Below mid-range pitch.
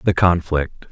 Yes: very low, 85 Hz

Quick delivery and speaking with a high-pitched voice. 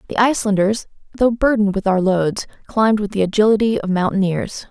No: average, 165 wpm; high, 205 Hz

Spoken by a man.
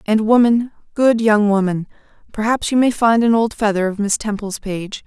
No: female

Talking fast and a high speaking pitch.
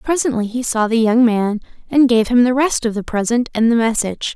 Yes: fast, 235 wpm; high, 235 Hz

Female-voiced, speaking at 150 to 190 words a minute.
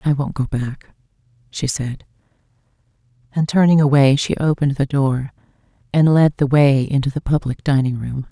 Yes: female; average, 160 wpm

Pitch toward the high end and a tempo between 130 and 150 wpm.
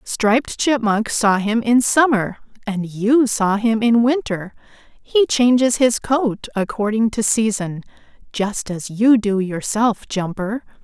Yes: high, 220 Hz; average, 140 wpm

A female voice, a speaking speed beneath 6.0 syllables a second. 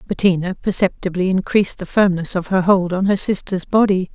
Yes: female; 5.6 syllables/s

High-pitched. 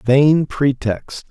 No: low, 135 Hz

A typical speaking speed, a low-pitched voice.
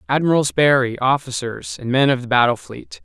Yes: average, 180 wpm; low, 130 Hz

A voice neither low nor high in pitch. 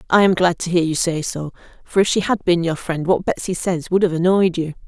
Yes: medium, 175 Hz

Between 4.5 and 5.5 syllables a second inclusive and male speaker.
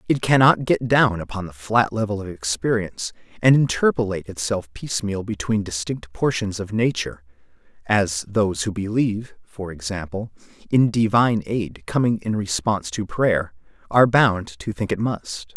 Yes: 5.0 syllables/s; male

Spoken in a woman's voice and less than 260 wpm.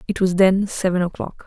Yes: female; fast, 205 wpm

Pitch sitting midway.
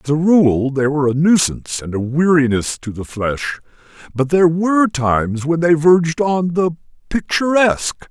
Yes: medium, 155 Hz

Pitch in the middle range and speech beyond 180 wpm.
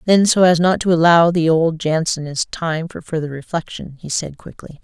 Yes: medium, 165 Hz; average, 200 wpm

